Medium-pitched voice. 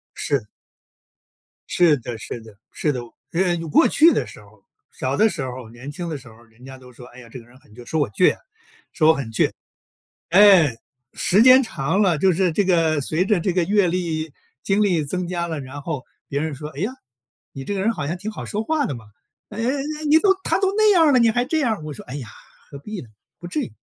Yes: medium, 165 Hz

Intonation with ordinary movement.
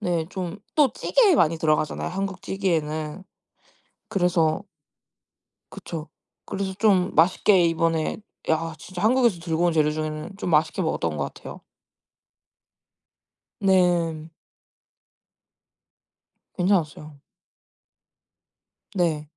Yes: average, 3.4 semitones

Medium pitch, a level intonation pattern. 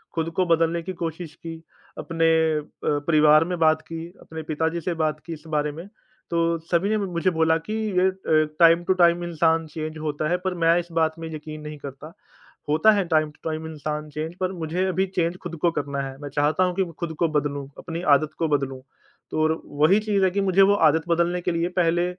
Yes: medium, 165 Hz; narrow, 2.0 semitones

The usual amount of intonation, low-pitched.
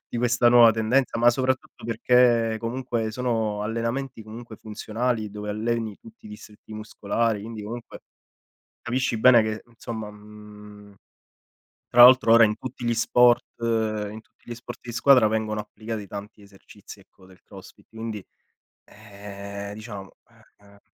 No: narrow, 2.2 semitones; low, 110 Hz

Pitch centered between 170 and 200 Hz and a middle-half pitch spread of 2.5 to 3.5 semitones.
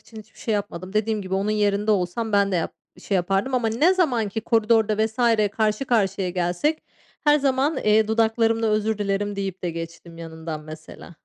No: high, 210 Hz; average, 3.1 semitones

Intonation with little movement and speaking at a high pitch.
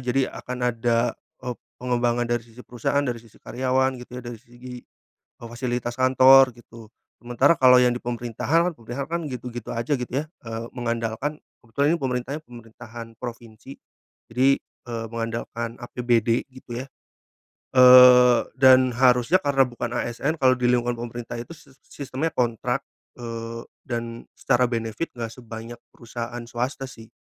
No: narrow, 1.6 semitones; low, 120 Hz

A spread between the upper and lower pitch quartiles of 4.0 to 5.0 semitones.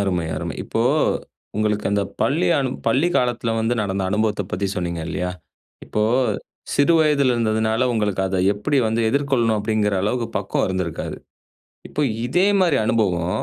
Yes: average, 4.3 semitones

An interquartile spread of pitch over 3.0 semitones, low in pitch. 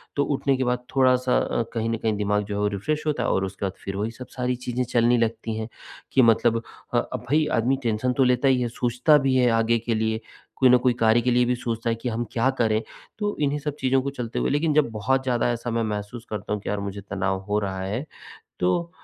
No: average, 2.7 semitones; low, 120 Hz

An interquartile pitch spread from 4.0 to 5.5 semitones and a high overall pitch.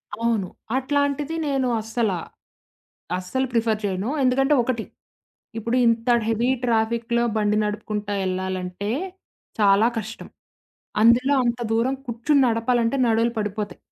No: average, 2.9 semitones; high, 230 Hz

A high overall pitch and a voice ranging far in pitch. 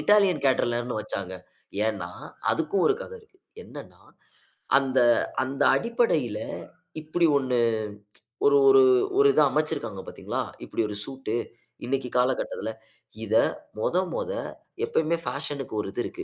No: low, 135 Hz; wide, 7.8 semitones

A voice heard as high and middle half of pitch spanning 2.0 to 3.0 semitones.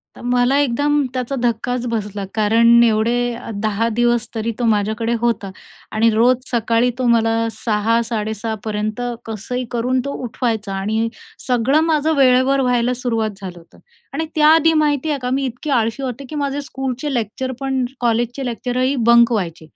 Yes: high, 240 Hz; narrow, 2.6 semitones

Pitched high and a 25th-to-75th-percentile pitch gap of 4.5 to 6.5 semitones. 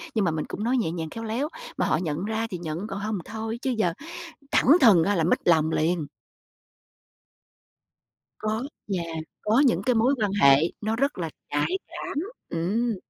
Yes: high, 205 Hz; average, 5.3 semitones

